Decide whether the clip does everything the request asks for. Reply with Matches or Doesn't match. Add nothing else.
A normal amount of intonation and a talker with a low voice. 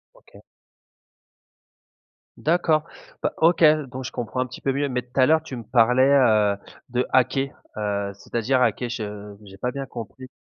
Matches